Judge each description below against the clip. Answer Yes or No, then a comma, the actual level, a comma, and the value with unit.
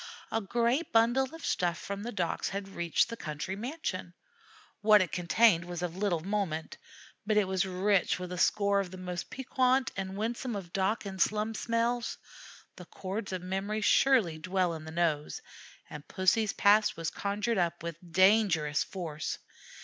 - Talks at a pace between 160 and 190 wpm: Yes, average, 170 wpm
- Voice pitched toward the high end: Yes, high, 195 Hz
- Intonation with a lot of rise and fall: No, average, 3.8 semitones